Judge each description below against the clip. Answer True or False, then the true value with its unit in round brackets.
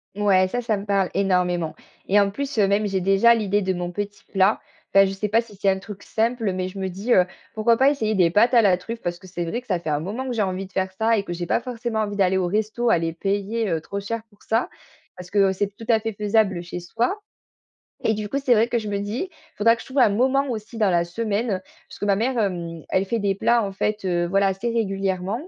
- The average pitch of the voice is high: True (205 Hz)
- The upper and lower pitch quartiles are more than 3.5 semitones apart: False (3.2 semitones)